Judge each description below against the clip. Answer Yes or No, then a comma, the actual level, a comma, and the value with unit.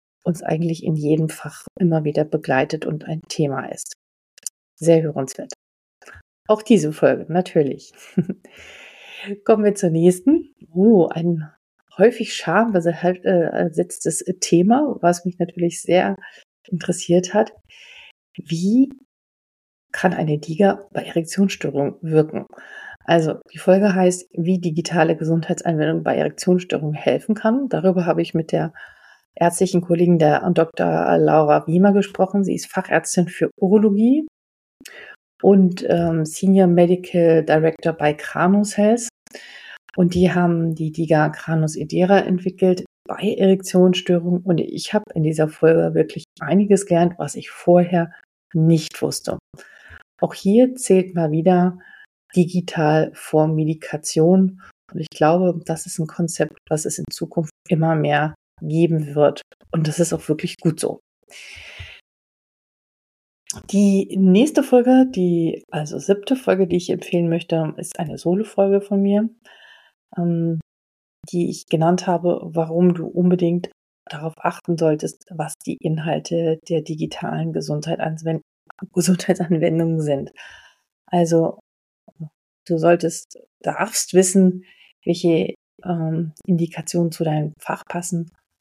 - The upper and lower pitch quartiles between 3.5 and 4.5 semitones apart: No, average, 2.8 semitones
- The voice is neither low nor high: Yes, medium, 175 Hz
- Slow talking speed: Yes, slow, 120 wpm